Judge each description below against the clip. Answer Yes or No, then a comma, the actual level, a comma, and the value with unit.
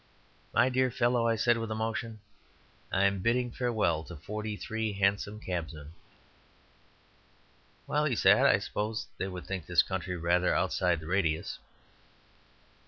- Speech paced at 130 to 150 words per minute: Yes, average, 140 wpm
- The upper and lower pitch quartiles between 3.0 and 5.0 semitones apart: Yes, average, 4.4 semitones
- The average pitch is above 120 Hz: No, low, 100 Hz